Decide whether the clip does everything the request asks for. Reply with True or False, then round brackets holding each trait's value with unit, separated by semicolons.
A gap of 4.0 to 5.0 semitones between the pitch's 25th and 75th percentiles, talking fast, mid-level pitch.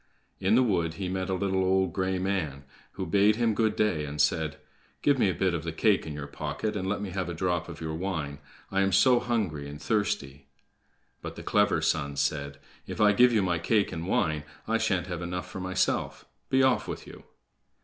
False (4.4 semitones; 220 wpm; 95 Hz)